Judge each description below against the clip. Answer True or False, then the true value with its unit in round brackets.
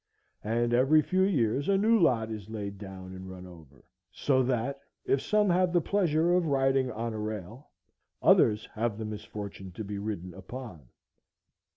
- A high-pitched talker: False (115 Hz)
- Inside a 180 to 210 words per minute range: False (170 wpm)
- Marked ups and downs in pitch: True (5.8 semitones)